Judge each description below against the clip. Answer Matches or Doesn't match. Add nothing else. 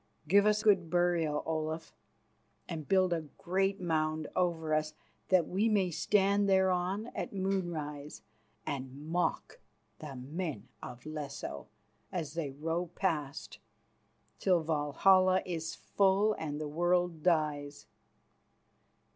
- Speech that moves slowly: Matches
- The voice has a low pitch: Doesn't match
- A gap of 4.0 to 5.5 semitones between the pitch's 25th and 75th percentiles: Doesn't match